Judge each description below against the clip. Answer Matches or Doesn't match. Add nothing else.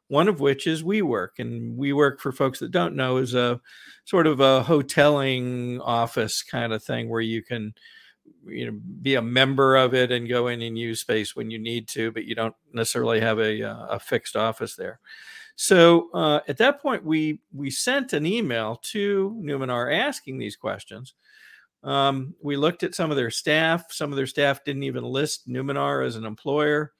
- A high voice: Doesn't match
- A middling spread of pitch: Matches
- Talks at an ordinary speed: Matches